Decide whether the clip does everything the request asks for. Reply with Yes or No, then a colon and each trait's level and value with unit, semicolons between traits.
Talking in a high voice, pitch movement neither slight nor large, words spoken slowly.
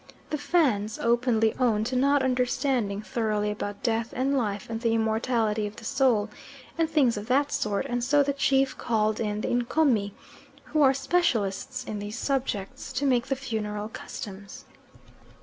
No: high, 235 Hz; average, 4.1 semitones; average, 165 wpm